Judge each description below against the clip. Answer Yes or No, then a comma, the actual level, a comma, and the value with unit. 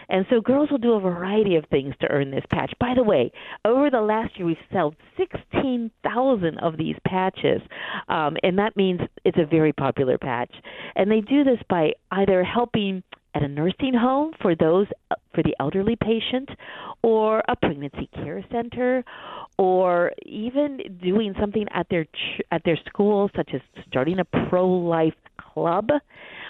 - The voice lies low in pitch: No, high, 195 Hz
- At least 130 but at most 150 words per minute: No, average, 175 wpm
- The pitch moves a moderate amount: No, wide, 5.8 semitones